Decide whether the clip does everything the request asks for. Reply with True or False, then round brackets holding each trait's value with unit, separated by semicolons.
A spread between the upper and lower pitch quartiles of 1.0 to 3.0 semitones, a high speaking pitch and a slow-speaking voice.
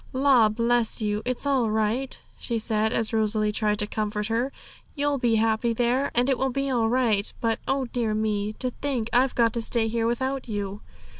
False (2.7 semitones; 230 Hz; 200 wpm)